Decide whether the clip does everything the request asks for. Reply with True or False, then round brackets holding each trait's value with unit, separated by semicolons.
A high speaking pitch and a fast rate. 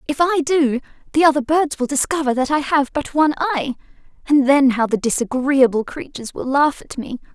False (280 Hz; 195 wpm)